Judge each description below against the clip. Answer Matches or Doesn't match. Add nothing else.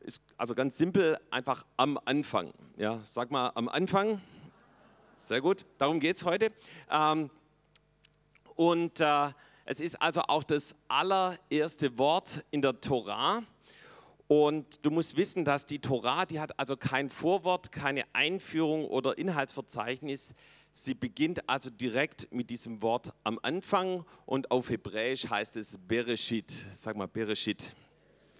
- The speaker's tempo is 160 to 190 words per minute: Doesn't match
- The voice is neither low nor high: Matches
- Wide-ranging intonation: Doesn't match